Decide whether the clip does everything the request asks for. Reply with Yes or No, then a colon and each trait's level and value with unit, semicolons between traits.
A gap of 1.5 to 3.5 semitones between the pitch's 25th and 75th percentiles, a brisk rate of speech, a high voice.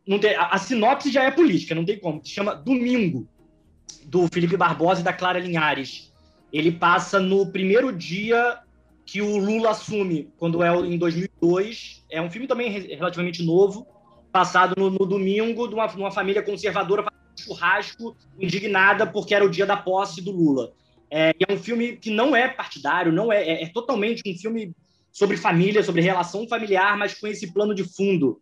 Yes: average, 3.2 semitones; fast, 190 wpm; high, 195 Hz